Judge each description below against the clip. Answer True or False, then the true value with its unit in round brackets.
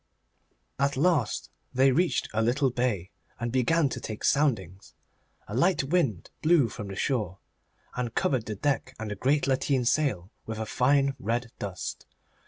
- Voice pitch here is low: True (125 Hz)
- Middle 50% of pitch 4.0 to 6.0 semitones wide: True (4.3 semitones)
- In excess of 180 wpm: False (160 wpm)